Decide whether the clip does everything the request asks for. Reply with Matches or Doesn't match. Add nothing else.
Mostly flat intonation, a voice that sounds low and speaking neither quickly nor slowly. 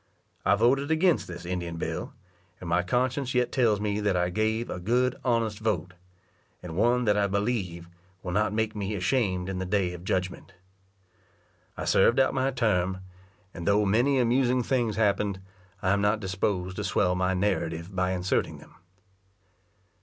Doesn't match